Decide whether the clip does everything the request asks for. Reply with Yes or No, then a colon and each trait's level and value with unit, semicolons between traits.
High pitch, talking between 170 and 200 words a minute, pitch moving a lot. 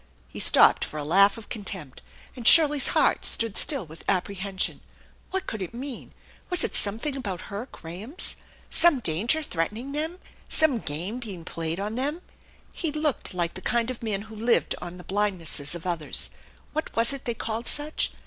Yes: high, 220 Hz; average, 180 wpm; wide, 6.9 semitones